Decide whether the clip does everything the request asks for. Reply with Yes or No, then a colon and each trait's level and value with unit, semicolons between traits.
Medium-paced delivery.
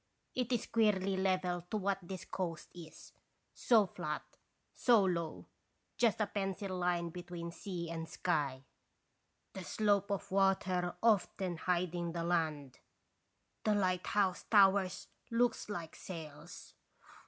No: slow, 125 wpm